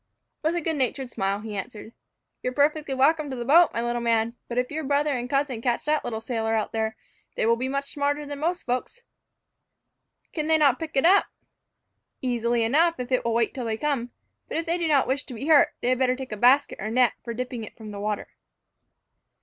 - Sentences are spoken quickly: Yes, fast, 230 wpm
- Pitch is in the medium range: No, very high, 255 Hz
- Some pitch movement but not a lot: Yes, average, 4.1 semitones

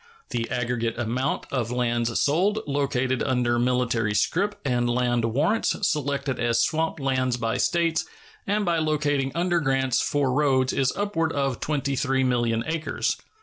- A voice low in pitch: Yes, low, 130 Hz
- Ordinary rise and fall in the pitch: Yes, average, 4.0 semitones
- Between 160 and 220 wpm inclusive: No, average, 140 wpm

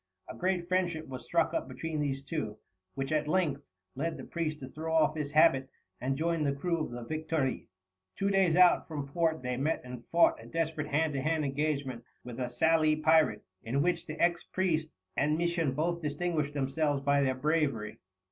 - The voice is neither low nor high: Yes, medium, 155 Hz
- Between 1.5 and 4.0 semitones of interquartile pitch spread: Yes, average, 3.2 semitones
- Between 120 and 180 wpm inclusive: No, average, 195 wpm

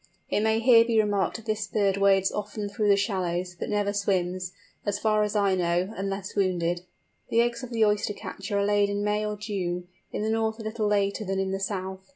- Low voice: No, high, 205 Hz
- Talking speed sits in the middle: No, fast, 220 wpm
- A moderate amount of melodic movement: No, narrow, 1.8 semitones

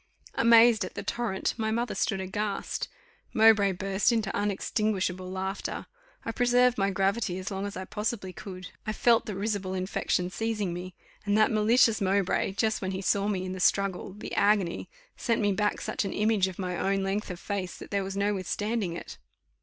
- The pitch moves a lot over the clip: No, narrow, 2.4 semitones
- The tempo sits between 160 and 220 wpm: Yes, average, 190 wpm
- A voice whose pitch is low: No, high, 200 Hz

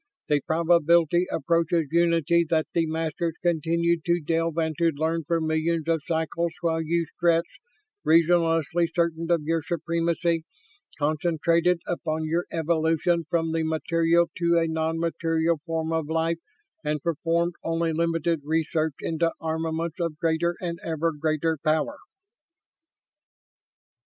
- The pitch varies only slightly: Yes, narrow, 0.9 semitones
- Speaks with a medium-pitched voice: Yes, medium, 165 Hz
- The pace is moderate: No, slow, 130 wpm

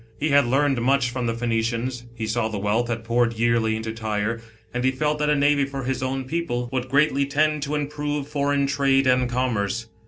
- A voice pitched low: Yes, low, 130 Hz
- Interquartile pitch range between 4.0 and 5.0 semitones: No, average, 3.4 semitones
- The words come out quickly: Yes, fast, 220 wpm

